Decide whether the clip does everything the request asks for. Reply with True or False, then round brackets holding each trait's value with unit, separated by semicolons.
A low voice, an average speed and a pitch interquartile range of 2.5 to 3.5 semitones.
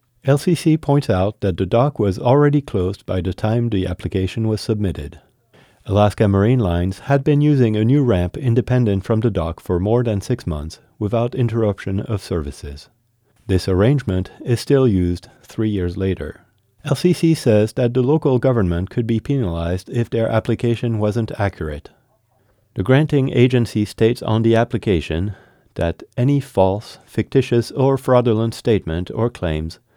False (115 Hz; 150 wpm; 4.8 semitones)